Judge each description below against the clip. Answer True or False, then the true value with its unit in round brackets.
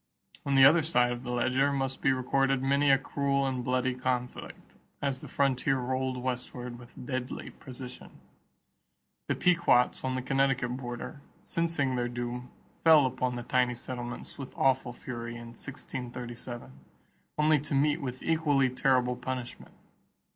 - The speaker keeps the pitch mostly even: True (1.8 semitones)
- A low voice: True (130 Hz)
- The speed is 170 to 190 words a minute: False (145 wpm)